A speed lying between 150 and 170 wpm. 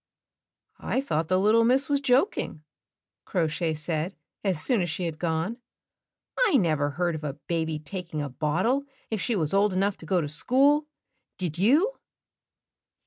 Yes: average, 165 wpm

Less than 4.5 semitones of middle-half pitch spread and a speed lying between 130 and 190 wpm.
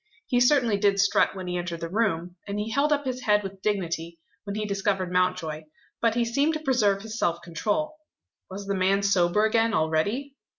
No: average, 4.1 semitones; average, 200 wpm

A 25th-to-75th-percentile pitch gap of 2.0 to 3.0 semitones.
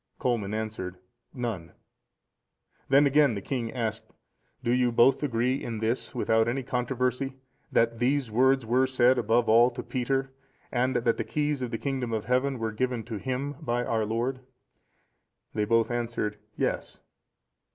Yes: narrow, 2.4 semitones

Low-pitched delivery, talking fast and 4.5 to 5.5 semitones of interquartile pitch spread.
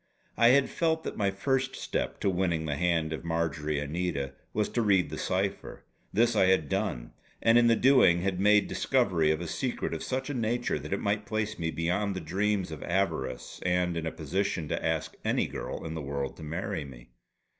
Yes: very low, 95 Hz; fast, 210 wpm; average, 4.9 semitones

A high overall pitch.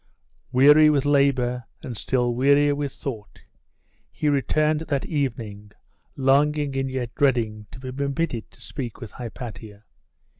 No: low, 135 Hz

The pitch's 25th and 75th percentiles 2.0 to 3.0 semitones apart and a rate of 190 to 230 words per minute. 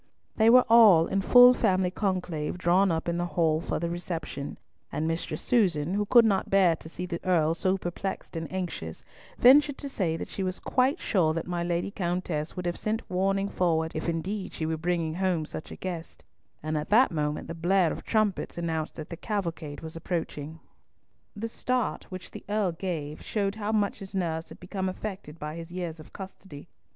No: average, 3.4 semitones; average, 200 wpm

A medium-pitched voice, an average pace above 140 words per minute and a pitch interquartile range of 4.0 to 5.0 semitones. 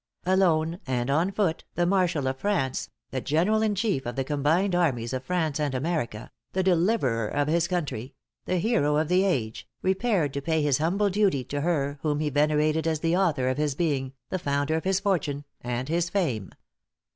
Yes: medium, 155 Hz; average, 190 wpm; average, 4.7 semitones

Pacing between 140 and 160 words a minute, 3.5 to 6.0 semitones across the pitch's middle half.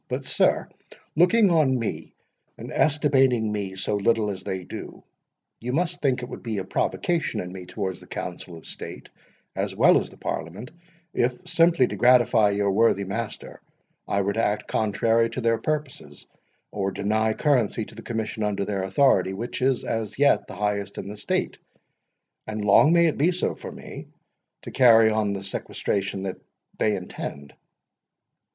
No: average, 170 wpm; average, 4.2 semitones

